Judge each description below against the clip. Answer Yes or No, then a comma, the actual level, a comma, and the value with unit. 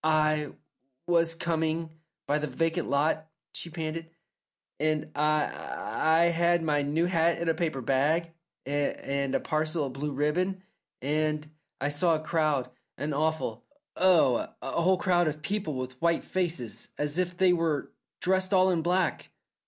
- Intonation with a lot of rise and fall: No, narrow, 2.5 semitones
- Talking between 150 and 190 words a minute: Yes, average, 155 wpm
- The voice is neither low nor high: Yes, medium, 160 Hz